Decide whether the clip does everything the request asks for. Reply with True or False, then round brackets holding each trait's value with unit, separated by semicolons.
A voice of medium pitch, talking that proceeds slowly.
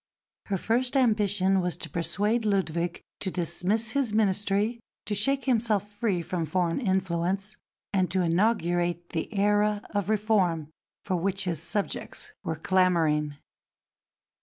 False (195 Hz; 130 wpm)